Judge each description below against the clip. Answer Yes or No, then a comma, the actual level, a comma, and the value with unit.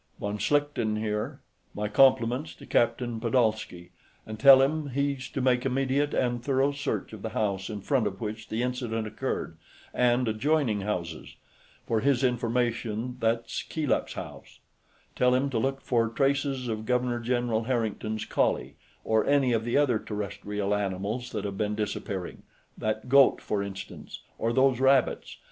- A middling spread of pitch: Yes, average, 3.5 semitones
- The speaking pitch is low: Yes, low, 120 Hz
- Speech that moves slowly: No, average, 155 wpm